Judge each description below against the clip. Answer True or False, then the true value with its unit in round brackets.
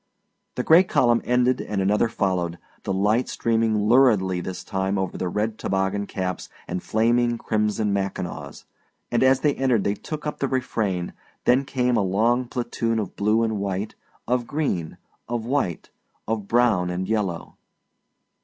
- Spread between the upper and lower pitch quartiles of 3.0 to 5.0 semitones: True (4.1 semitones)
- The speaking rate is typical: True (155 wpm)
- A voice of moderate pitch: False (110 Hz)